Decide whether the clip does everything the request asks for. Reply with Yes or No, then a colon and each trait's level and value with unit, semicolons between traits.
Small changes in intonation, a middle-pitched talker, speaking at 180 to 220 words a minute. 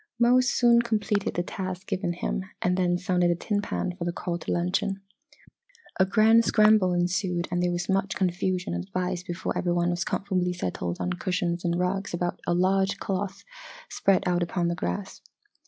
Yes: narrow, 1.9 semitones; medium, 180 Hz; average, 185 wpm